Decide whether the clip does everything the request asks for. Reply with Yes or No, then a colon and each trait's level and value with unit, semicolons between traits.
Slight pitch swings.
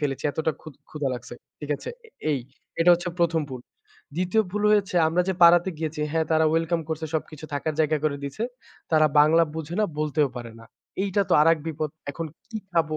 Yes: narrow, 2.2 semitones